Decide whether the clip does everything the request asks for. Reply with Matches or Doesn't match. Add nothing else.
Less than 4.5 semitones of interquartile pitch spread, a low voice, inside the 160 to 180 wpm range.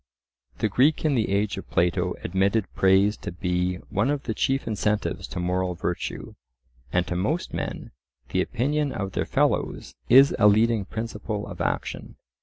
Matches